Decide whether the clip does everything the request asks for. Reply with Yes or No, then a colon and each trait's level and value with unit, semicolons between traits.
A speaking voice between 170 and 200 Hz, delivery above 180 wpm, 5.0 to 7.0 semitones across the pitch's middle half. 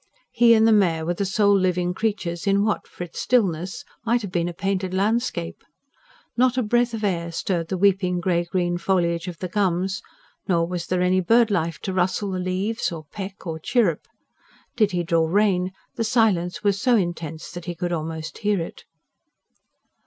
No: medium, 185 Hz; average, 190 wpm; average, 3.1 semitones